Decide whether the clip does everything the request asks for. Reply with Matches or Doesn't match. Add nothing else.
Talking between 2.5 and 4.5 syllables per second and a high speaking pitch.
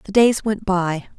Matches